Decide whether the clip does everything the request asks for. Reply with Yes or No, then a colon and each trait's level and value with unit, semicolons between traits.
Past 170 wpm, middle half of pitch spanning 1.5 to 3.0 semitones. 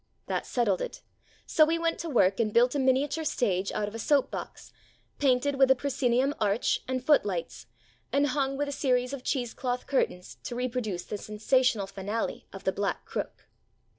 No: average, 190 wpm; average, 4.8 semitones